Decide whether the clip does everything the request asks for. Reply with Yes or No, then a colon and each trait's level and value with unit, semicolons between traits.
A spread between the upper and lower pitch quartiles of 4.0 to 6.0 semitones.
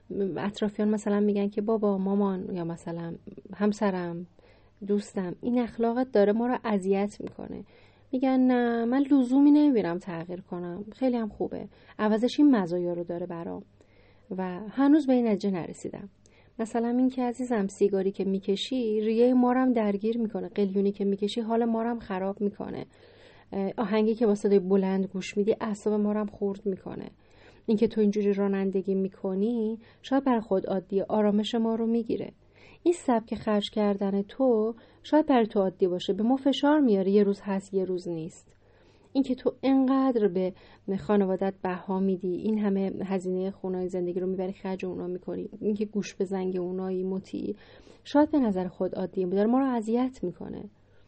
No: average, 3.4 semitones